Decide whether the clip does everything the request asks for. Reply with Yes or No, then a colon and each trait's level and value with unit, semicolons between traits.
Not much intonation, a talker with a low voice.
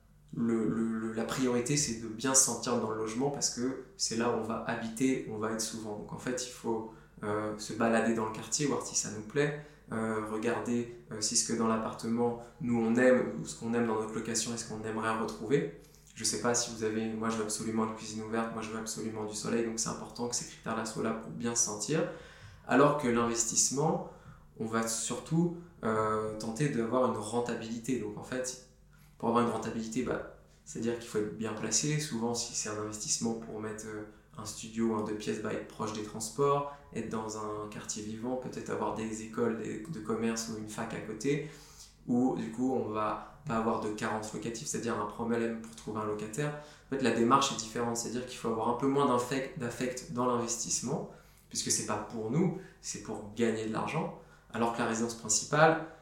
Yes: narrow, 1.9 semitones; low, 115 Hz